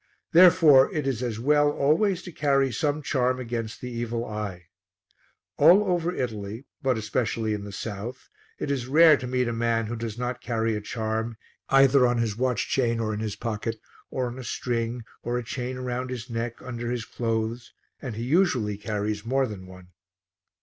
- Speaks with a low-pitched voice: Yes, low, 120 Hz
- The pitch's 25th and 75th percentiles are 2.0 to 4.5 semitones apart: Yes, average, 2.9 semitones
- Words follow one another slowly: No, average, 185 wpm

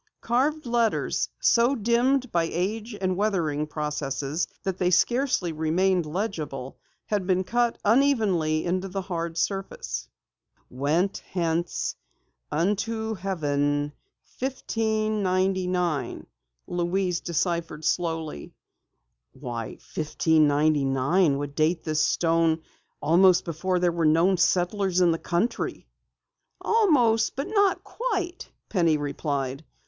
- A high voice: No, medium, 180 Hz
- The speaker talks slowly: Yes, slow, 100 wpm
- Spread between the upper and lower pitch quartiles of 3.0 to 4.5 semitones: No, wide, 5.4 semitones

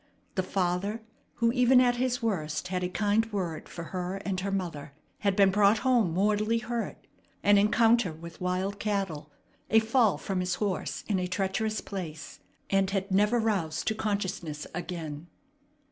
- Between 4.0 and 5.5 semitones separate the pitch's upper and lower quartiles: No, average, 3.3 semitones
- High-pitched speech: Yes, high, 195 Hz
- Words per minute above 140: Yes, average, 160 wpm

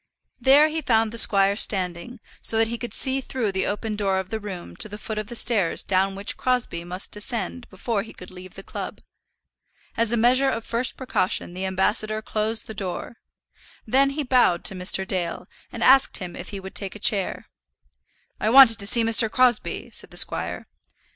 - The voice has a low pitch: No, high, 215 Hz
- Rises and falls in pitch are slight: No, average, 3.8 semitones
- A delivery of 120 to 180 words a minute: No, average, 200 wpm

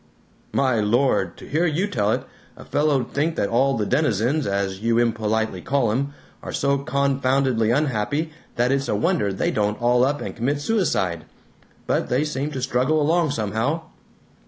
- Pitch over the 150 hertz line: No, low, 130 Hz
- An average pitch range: Yes, average, 4.5 semitones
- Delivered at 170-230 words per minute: Yes, average, 175 wpm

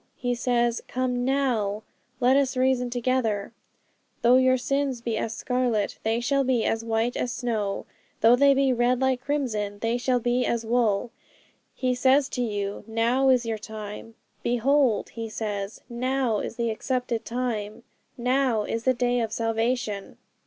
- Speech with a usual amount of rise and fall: No, narrow, 2.3 semitones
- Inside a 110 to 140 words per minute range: No, average, 160 wpm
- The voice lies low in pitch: No, high, 240 Hz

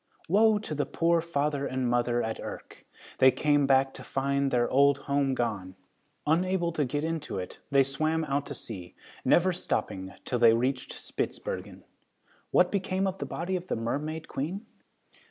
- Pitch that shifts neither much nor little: Yes, average, 4.5 semitones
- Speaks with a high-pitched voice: No, medium, 140 Hz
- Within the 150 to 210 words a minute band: Yes, average, 170 wpm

